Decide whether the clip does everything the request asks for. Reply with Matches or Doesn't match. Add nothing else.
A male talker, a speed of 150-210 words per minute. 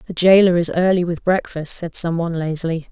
Doesn't match